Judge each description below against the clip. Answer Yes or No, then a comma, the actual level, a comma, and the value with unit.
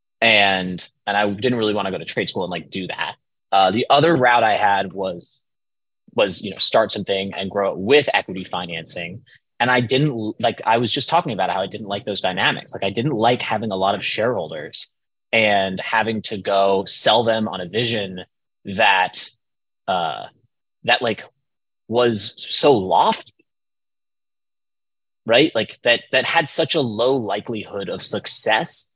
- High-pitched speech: No, low, 105 Hz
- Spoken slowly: No, average, 175 wpm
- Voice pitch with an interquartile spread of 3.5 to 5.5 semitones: No, average, 2.9 semitones